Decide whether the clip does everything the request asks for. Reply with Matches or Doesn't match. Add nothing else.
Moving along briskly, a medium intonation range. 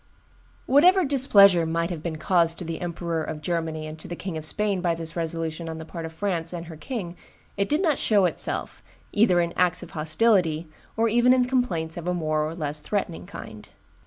Matches